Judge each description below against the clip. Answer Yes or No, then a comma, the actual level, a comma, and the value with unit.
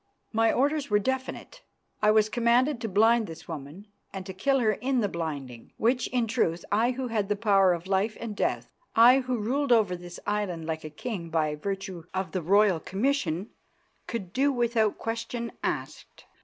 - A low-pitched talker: No, high, 210 Hz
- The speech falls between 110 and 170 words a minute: No, average, 180 wpm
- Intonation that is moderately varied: Yes, average, 4.7 semitones